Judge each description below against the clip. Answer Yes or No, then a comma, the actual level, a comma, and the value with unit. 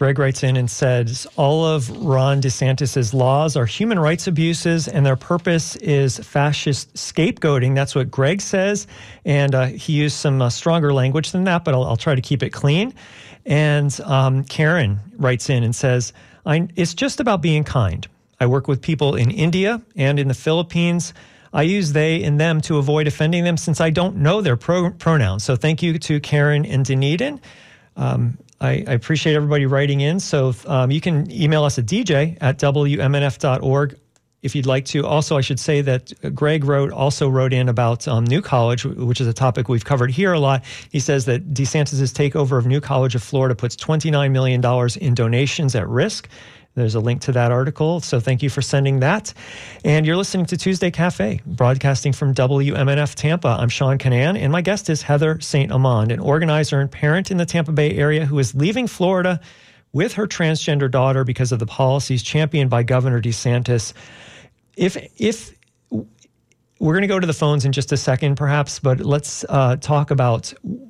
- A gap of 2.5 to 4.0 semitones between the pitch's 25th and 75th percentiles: Yes, average, 3.4 semitones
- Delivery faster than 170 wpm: Yes, average, 190 wpm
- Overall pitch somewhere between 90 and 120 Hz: No, medium, 140 Hz